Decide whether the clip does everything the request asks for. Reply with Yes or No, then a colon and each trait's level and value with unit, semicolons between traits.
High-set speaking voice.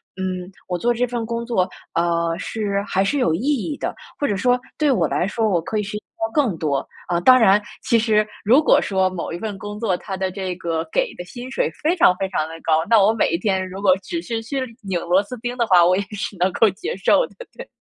Yes: high, 200 Hz